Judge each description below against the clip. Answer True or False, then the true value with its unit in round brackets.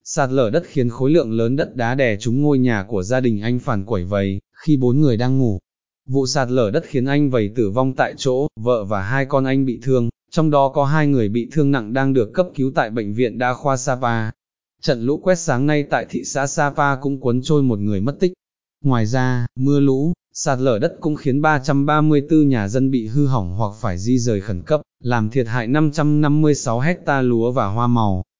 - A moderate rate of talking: True (225 wpm)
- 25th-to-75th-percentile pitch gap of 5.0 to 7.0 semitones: False (3.5 semitones)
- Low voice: True (130 Hz)